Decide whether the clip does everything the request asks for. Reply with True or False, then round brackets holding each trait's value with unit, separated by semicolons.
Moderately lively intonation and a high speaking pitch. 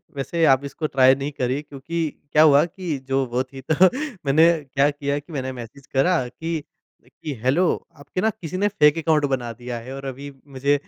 False (3.2 semitones; 140 Hz)